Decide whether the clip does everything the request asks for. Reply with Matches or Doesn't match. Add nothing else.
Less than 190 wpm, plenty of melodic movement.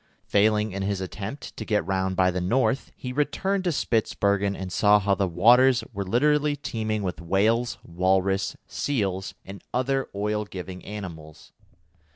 Doesn't match